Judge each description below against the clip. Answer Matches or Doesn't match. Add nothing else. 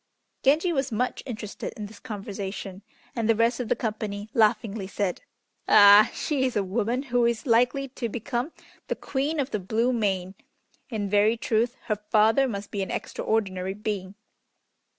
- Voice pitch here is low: Doesn't match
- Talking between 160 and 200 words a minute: Matches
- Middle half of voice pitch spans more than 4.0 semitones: Doesn't match